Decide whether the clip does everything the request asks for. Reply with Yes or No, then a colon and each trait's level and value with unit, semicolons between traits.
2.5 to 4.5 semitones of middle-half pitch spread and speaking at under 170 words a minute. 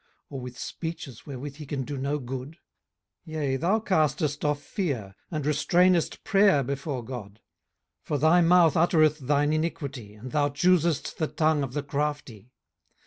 Yes: average, 3.2 semitones; average, 160 wpm